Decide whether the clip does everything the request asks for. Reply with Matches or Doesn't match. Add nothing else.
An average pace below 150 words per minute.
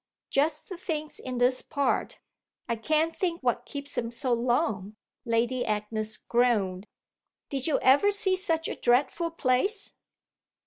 Matches